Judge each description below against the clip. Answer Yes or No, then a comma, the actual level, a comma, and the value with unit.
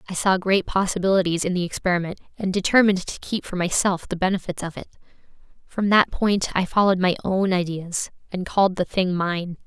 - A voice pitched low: No, medium, 185 Hz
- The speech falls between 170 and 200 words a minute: Yes, average, 185 wpm